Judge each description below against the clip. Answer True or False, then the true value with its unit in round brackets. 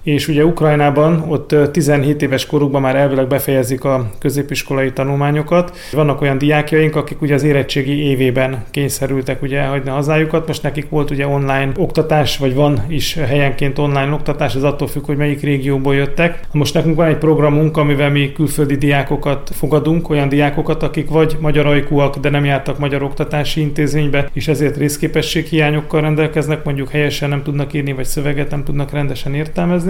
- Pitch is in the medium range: True (145 Hz)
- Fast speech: True (165 wpm)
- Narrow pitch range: True (1.4 semitones)